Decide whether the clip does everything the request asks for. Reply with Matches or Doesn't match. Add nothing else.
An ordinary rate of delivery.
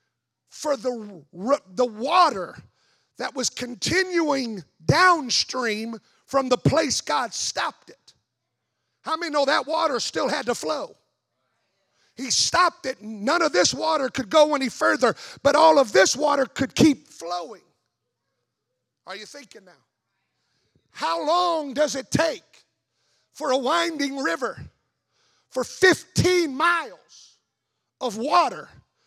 Doesn't match